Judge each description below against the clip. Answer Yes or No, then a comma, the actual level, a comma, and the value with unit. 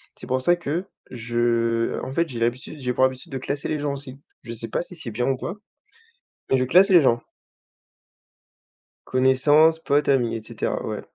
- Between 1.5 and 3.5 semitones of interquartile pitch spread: No, average, 3.9 semitones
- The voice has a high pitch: No, low, 130 Hz